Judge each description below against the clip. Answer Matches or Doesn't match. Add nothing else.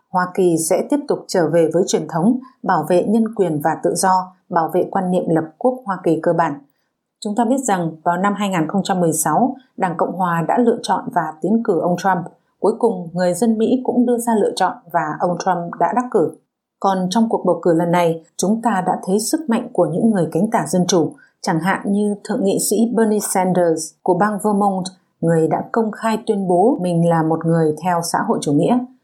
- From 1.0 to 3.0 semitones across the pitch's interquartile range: Doesn't match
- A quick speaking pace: Matches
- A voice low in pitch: Doesn't match